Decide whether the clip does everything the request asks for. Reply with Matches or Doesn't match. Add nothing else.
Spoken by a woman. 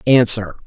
Doesn't match